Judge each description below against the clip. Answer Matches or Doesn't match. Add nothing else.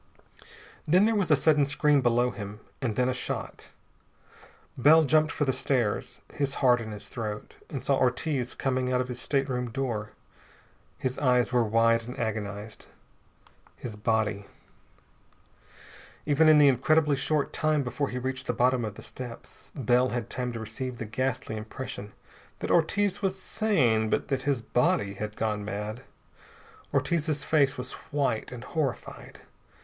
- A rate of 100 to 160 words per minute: Matches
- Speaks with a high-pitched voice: Doesn't match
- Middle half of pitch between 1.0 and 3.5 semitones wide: Doesn't match